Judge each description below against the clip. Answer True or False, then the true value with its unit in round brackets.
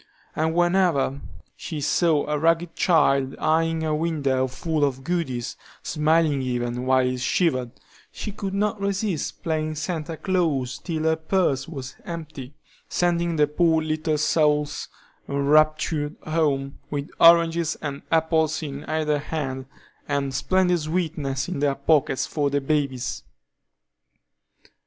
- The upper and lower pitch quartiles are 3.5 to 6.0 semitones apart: False (3.0 semitones)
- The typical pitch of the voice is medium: True (155 Hz)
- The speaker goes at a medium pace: False (130 wpm)